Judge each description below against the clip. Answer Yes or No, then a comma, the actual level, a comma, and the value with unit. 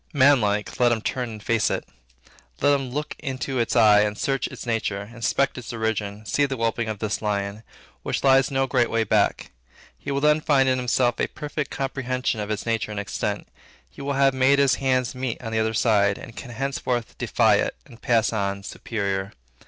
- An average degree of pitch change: Yes, average, 3.8 semitones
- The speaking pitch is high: No, low, 120 Hz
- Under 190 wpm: No, average, 200 wpm